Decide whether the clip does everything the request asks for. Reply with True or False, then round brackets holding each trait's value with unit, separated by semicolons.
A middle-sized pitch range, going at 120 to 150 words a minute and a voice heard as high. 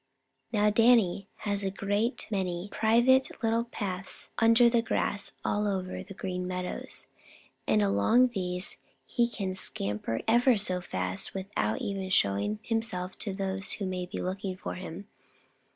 True (3.7 semitones; 145 wpm; 195 Hz)